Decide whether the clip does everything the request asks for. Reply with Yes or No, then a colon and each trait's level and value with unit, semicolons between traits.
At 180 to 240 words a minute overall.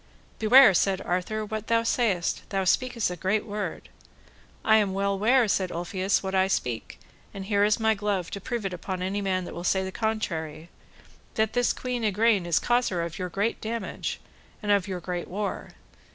Yes: average, 190 wpm